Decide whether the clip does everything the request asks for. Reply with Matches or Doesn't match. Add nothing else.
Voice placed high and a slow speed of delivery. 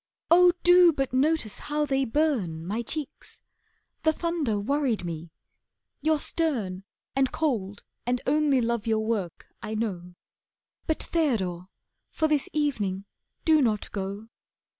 Matches